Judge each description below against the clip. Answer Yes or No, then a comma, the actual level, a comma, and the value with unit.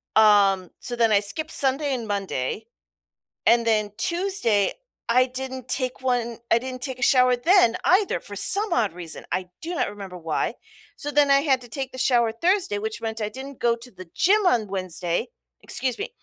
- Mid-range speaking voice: No, high, 240 Hz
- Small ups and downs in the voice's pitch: No, average, 4.5 semitones